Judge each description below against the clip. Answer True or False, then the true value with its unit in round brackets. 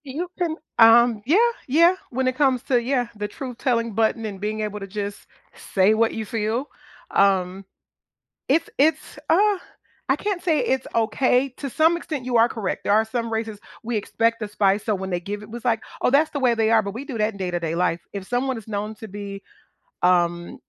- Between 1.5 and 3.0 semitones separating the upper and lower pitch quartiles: False (4.2 semitones)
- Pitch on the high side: True (225 Hz)